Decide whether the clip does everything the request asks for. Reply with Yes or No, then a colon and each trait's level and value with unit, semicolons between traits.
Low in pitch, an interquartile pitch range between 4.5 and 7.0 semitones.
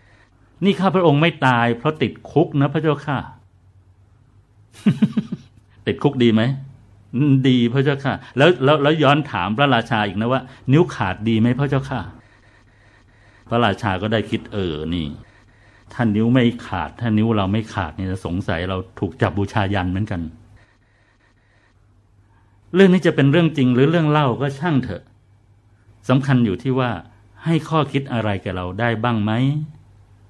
Yes: low, 110 Hz; average, 4.9 semitones